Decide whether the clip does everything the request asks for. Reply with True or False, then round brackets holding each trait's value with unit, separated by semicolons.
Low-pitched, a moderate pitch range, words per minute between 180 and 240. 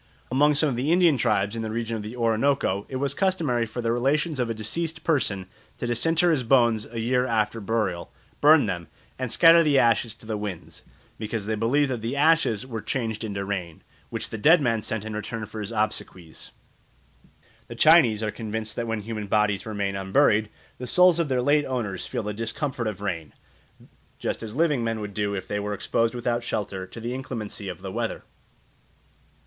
True (115 Hz; 4.0 semitones; 200 wpm)